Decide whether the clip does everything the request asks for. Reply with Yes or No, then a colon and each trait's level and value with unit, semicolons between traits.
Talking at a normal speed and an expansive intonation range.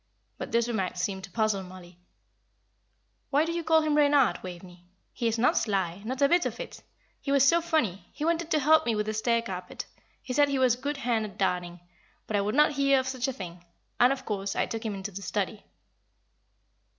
No: fast, 225 wpm; wide, 6.4 semitones